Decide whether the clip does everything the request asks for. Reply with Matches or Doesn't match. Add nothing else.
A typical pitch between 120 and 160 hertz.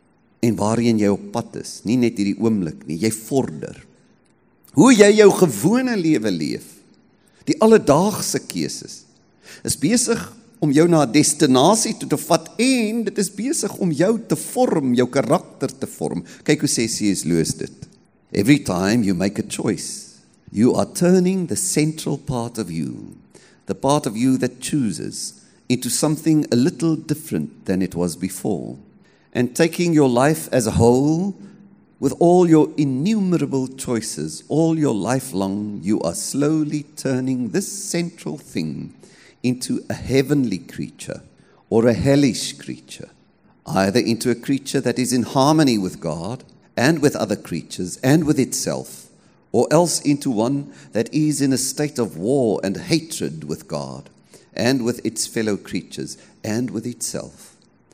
Matches